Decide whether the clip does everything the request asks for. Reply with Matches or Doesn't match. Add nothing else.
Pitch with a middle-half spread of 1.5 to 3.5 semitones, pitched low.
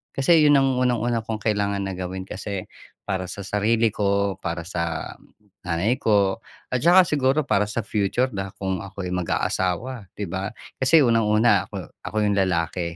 Doesn't match